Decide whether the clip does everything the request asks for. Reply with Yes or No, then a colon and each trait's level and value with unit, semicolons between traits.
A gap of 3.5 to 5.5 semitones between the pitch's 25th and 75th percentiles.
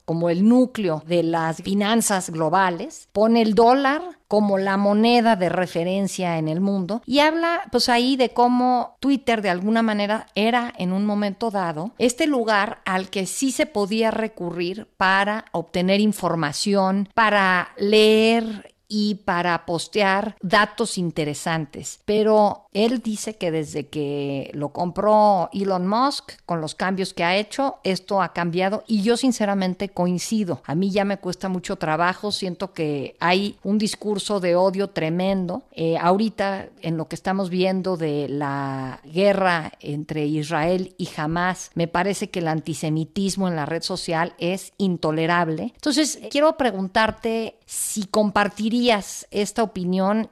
Yes: average, 3.9 semitones